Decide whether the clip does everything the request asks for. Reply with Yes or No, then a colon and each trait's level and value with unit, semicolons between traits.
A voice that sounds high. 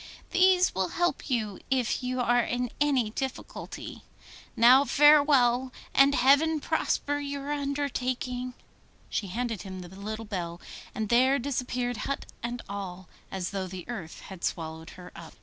Yes: high, 245 Hz